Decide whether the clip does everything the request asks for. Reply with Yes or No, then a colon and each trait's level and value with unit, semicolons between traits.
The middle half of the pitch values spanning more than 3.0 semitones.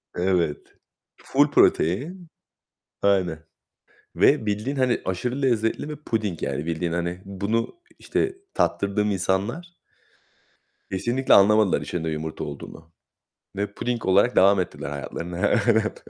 Yes: average, 5.3 semitones